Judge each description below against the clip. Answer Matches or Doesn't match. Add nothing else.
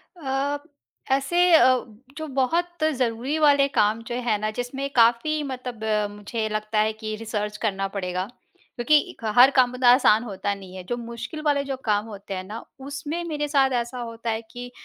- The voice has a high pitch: Matches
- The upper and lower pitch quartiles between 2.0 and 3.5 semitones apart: Doesn't match